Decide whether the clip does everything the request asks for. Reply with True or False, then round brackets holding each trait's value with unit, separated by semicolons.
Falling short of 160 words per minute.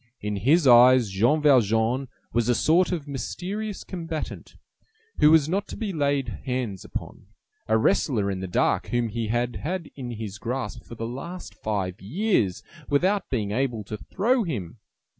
False (165 wpm)